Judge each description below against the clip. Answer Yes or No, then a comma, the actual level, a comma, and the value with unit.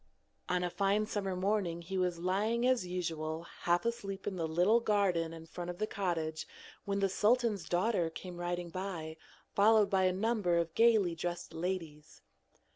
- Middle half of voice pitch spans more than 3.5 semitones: No, average, 3.1 semitones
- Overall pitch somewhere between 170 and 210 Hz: Yes, medium, 185 Hz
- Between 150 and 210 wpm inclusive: Yes, average, 170 wpm